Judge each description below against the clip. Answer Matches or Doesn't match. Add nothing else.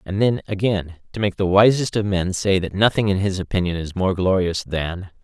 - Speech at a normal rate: Doesn't match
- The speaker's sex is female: Doesn't match